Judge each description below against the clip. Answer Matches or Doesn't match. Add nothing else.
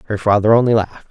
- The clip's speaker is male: Matches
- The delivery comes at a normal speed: Doesn't match